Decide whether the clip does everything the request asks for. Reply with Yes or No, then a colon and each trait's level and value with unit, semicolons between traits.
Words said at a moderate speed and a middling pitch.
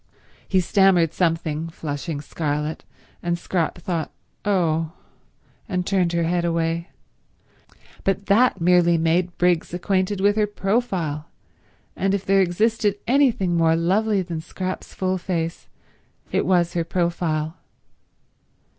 No: slow, 120 wpm; medium, 175 Hz